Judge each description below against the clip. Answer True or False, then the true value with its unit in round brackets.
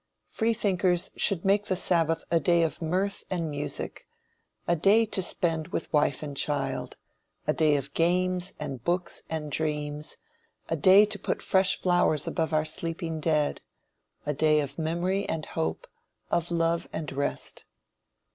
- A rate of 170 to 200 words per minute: False (155 wpm)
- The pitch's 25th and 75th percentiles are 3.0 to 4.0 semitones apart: True (3.3 semitones)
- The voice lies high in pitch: False (165 Hz)